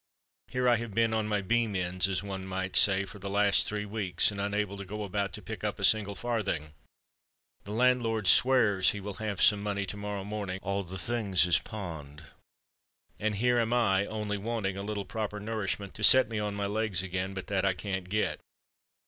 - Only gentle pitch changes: Yes, narrow, 2.1 semitones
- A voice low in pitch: Yes, low, 100 Hz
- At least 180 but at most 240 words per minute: Yes, average, 200 wpm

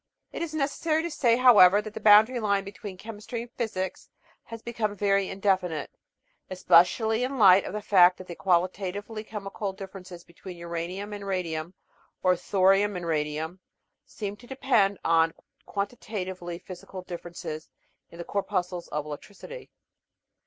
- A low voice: No, high, 195 Hz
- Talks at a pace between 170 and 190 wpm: No, average, 150 wpm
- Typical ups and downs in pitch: Yes, average, 3.2 semitones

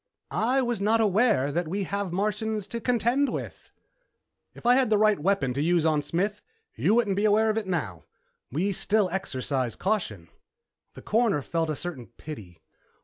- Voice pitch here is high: Yes, high, 200 Hz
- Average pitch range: No, wide, 5.9 semitones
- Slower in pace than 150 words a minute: No, average, 175 wpm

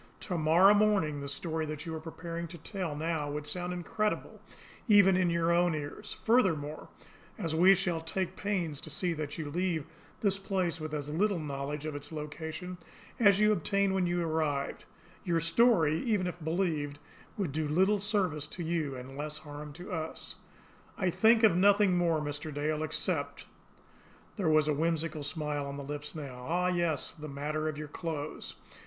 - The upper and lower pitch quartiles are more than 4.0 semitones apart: No, average, 3.4 semitones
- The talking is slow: No, average, 180 wpm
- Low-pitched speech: No, medium, 160 Hz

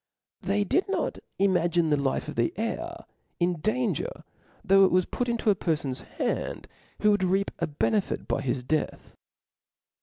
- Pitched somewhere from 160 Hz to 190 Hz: Yes, medium, 185 Hz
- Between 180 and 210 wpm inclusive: No, average, 160 wpm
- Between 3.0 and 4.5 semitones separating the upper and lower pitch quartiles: No, average, 5.2 semitones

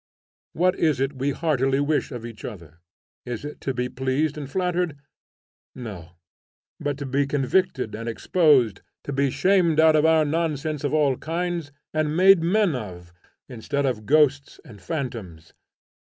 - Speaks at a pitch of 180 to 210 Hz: No, medium, 140 Hz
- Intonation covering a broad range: No, average, 4.2 semitones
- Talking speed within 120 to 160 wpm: Yes, average, 155 wpm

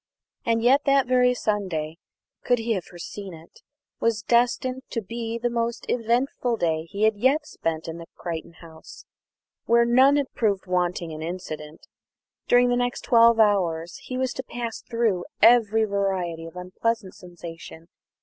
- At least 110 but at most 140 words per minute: No, average, 155 wpm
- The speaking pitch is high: Yes, high, 220 Hz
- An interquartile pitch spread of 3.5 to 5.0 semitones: No, wide, 5.5 semitones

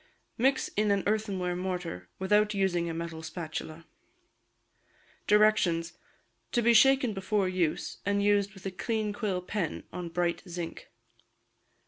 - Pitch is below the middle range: No, high, 190 Hz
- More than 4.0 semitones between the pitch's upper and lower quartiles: No, average, 3.4 semitones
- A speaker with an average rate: No, slow, 130 wpm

